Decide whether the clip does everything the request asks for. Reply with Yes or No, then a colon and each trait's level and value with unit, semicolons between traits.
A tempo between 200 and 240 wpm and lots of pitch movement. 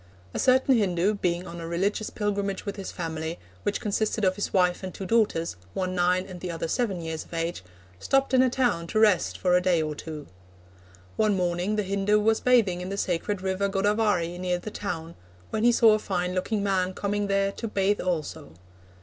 No: fast, 205 wpm; average, 2.9 semitones